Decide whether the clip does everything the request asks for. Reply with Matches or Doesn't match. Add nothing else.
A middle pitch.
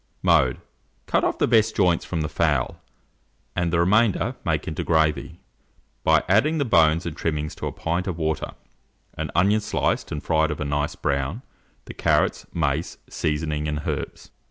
Doesn't match